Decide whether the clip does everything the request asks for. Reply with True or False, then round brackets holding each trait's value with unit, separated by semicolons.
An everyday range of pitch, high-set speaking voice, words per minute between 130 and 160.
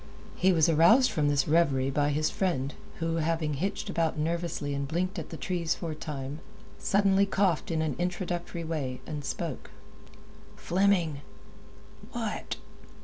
False (3.2 semitones; 165 Hz; 145 wpm)